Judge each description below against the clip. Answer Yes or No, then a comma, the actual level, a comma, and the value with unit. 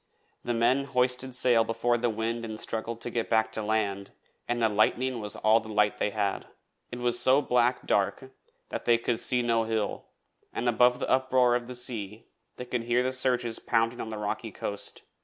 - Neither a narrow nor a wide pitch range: No, narrow, 1.9 semitones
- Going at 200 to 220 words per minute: Yes, fast, 205 wpm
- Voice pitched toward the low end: Yes, low, 115 Hz